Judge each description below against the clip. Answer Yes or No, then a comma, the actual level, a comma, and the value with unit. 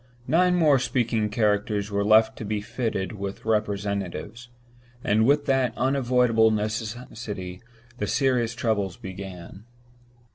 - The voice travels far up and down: No, average, 3.3 semitones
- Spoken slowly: Yes, slow, 115 wpm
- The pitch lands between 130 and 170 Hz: No, low, 110 Hz